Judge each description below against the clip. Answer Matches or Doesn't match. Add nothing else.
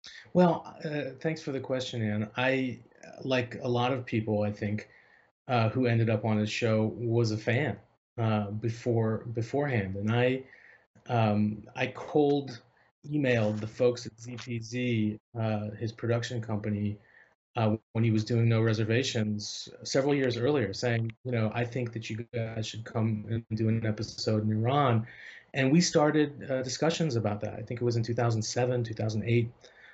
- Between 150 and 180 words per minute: Matches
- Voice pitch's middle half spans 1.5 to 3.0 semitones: Matches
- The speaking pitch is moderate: Doesn't match